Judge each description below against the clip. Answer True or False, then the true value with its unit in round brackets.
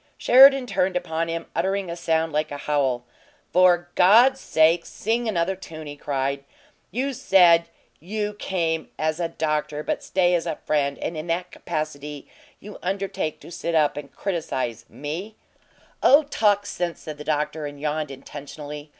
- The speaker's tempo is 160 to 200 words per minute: True (165 wpm)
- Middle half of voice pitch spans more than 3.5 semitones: True (4.1 semitones)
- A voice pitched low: False (165 Hz)